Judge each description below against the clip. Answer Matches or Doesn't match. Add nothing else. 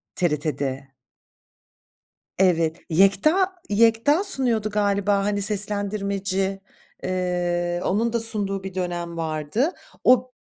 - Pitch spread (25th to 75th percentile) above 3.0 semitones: Matches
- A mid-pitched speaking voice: Doesn't match